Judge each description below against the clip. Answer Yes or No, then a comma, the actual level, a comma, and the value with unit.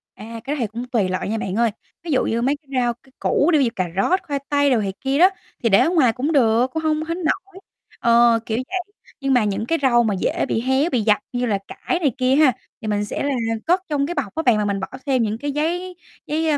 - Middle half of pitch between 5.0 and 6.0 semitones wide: Yes, average, 5.3 semitones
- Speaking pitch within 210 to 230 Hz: No, very high, 255 Hz